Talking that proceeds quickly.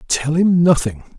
No: average, 150 wpm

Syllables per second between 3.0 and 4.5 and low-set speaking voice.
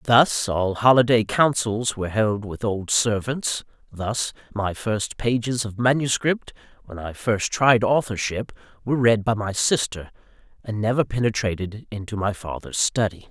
Yes: 4.4 syllables/s; low, 110 Hz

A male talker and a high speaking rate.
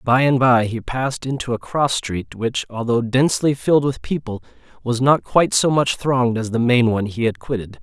Yes: male; fast, 215 wpm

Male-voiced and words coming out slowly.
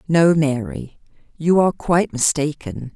No: female; slow, 120 wpm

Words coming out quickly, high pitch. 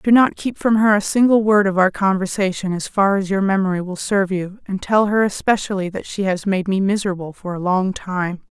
Yes: fast, 235 wpm; high, 195 Hz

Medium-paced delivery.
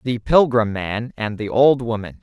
Yes: average, 190 wpm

